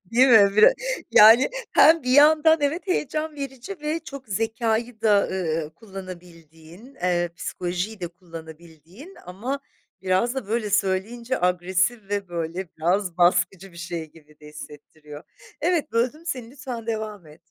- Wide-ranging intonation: Yes, wide, 6.3 semitones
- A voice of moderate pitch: No, high, 200 Hz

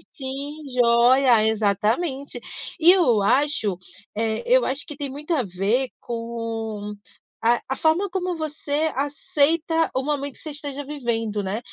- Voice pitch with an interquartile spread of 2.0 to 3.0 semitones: No, average, 4.7 semitones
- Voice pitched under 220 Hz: No, very high, 265 Hz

